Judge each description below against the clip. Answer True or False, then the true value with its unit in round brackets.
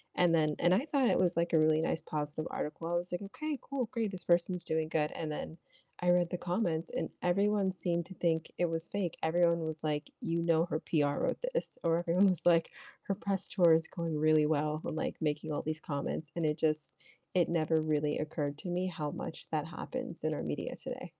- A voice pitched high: False (165 Hz)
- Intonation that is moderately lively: False (2.3 semitones)